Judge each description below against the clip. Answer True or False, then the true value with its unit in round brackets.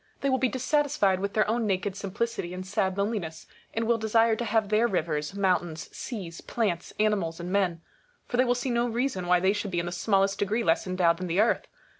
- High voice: True (200 Hz)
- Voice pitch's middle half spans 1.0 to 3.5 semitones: False (4.2 semitones)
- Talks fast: True (230 wpm)